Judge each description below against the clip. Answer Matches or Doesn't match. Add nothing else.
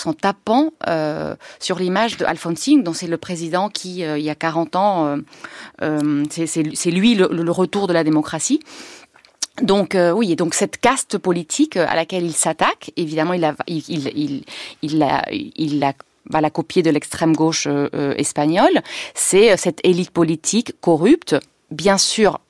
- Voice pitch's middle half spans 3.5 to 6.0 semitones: Matches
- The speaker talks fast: Doesn't match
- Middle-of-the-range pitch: Matches